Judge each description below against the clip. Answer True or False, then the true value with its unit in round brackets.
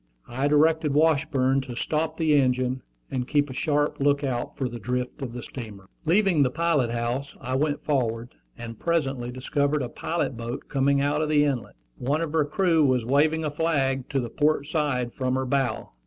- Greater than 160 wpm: True (190 wpm)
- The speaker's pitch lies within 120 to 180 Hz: True (140 Hz)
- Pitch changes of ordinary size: True (3.1 semitones)